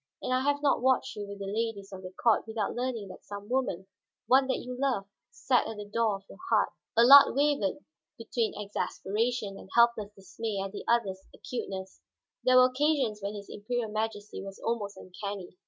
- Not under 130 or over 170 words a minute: No, average, 190 wpm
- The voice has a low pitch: No, high, 220 Hz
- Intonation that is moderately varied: Yes, average, 3.8 semitones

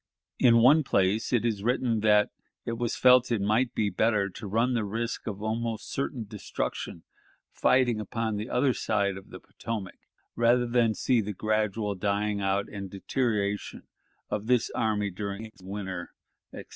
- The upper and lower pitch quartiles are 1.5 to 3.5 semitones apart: Yes, average, 2.7 semitones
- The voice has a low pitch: Yes, low, 110 Hz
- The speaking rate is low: No, average, 165 wpm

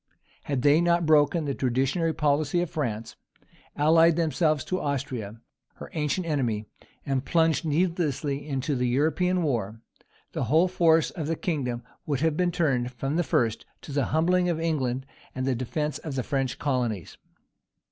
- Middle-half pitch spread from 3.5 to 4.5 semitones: Yes, average, 4.0 semitones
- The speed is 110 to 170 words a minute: Yes, average, 160 wpm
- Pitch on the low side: No, medium, 145 Hz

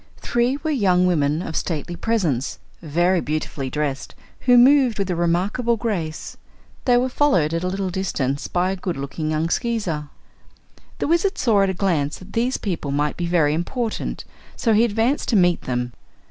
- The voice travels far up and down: Yes, wide, 6.7 semitones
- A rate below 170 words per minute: No, average, 175 wpm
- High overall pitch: No, medium, 180 Hz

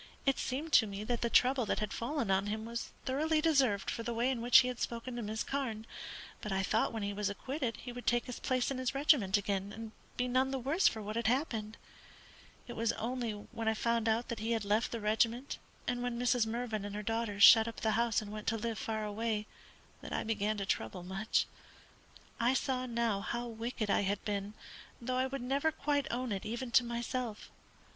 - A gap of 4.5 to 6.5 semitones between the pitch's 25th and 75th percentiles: No, average, 2.8 semitones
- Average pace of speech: No, fast, 225 wpm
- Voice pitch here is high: Yes, high, 230 Hz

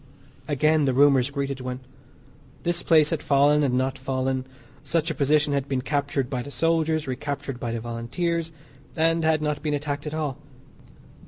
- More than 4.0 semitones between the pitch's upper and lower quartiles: No, average, 2.8 semitones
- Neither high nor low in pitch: Yes, medium, 145 Hz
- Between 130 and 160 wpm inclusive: No, average, 175 wpm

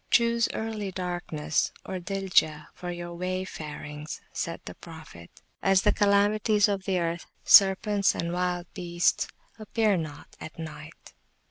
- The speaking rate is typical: No, slow, 125 wpm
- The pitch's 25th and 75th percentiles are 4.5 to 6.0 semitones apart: No, average, 3.3 semitones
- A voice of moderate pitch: Yes, medium, 180 Hz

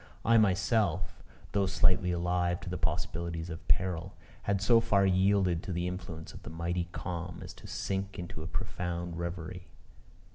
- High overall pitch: No, very low, 90 Hz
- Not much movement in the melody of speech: Yes, narrow, 2.0 semitones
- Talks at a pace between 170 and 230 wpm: No, average, 160 wpm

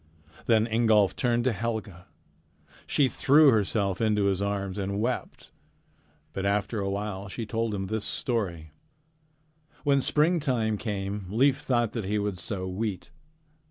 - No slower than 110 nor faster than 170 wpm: Yes, average, 140 wpm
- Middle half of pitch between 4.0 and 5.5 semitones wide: No, average, 3.1 semitones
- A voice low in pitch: Yes, low, 105 Hz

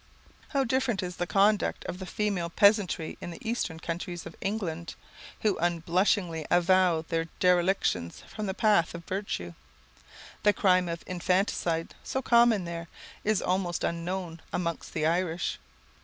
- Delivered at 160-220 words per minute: No, average, 140 wpm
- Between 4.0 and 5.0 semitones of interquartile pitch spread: No, average, 3.2 semitones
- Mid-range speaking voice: Yes, medium, 180 Hz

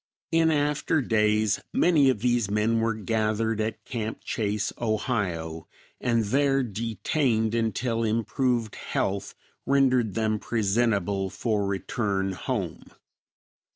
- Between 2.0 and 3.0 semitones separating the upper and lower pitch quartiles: Yes, average, 2.7 semitones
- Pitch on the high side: No, low, 110 Hz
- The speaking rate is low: Yes, slow, 110 wpm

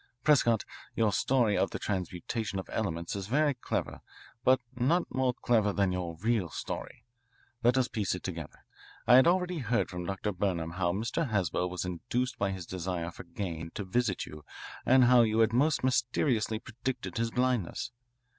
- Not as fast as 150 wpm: No, average, 175 wpm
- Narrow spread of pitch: No, average, 5.3 semitones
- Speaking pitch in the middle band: No, low, 110 Hz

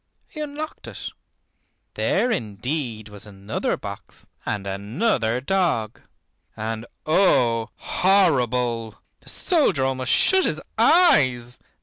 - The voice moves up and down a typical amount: No, wide, 9.0 semitones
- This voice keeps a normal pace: No, slow, 100 wpm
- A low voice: Yes, low, 125 Hz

